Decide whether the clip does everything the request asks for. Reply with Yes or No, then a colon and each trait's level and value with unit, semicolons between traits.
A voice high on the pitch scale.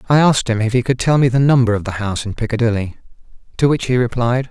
No: low, 120 Hz